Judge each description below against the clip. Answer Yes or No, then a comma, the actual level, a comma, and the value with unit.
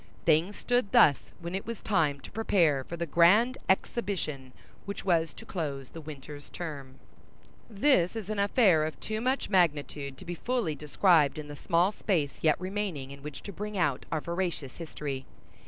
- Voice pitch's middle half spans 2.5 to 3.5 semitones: No, wide, 5.4 semitones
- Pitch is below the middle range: No, medium, 170 Hz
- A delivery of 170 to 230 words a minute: Yes, average, 175 wpm